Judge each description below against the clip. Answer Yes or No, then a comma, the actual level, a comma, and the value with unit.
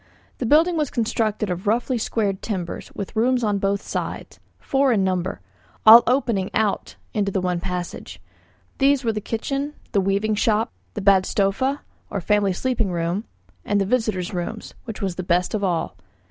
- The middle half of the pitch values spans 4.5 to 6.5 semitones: No, average, 3.6 semitones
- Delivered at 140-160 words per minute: No, average, 170 wpm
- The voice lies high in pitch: Yes, high, 210 Hz